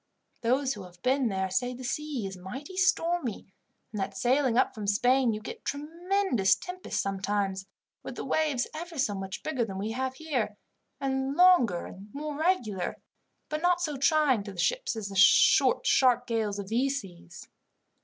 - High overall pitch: Yes, very high, 250 Hz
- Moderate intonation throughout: No, wide, 6.9 semitones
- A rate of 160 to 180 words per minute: Yes, average, 175 wpm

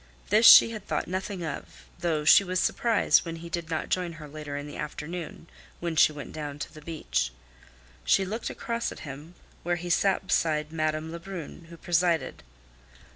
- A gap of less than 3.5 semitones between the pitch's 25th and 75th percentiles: Yes, average, 2.9 semitones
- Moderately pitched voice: Yes, medium, 165 Hz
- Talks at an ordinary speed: Yes, average, 180 wpm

